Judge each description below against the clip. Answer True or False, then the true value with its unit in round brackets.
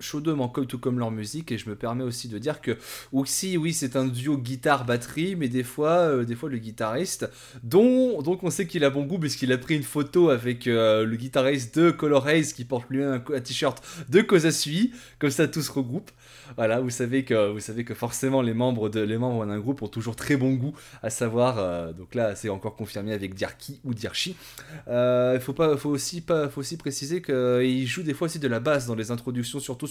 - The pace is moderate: False (225 wpm)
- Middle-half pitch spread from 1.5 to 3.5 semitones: False (4.0 semitones)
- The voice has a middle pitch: False (130 Hz)